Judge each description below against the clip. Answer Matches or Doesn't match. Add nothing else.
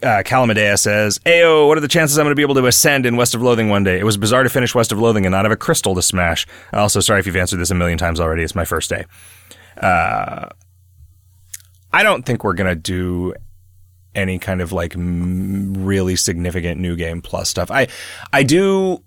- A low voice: Matches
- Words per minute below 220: Doesn't match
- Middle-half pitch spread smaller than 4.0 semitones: Doesn't match